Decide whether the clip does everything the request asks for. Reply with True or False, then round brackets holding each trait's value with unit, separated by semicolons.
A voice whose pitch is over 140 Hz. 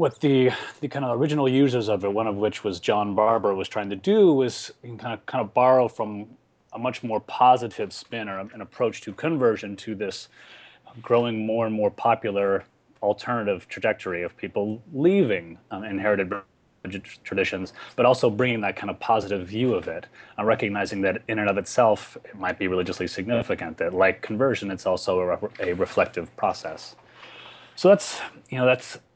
False (110 Hz)